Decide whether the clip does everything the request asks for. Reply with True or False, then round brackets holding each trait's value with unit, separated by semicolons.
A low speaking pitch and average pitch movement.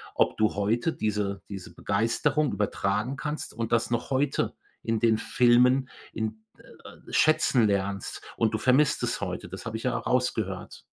True (115 Hz; 3.2 semitones)